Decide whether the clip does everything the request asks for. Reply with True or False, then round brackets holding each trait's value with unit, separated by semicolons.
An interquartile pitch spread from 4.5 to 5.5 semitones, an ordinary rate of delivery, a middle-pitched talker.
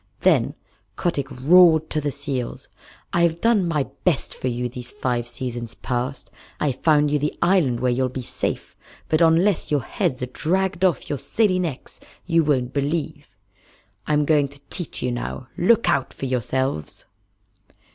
True (4.8 semitones; 160 wpm; 145 Hz)